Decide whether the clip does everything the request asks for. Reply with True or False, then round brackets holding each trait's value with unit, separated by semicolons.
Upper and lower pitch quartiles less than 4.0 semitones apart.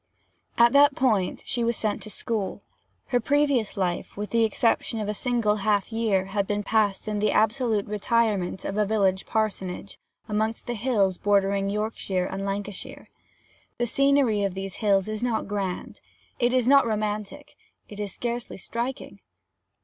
True (2.9 semitones)